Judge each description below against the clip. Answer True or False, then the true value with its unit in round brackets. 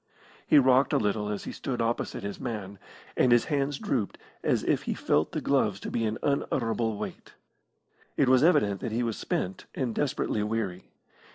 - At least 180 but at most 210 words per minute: True (185 wpm)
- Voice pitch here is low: True (115 Hz)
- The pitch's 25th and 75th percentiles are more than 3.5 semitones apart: True (4.0 semitones)